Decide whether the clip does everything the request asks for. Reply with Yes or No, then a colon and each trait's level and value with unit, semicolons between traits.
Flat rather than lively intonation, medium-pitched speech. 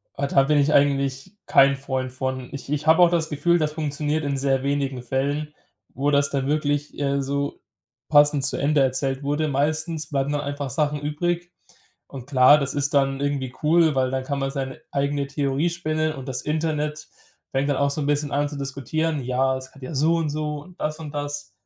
Yes: narrow, 1.8 semitones; medium, 145 Hz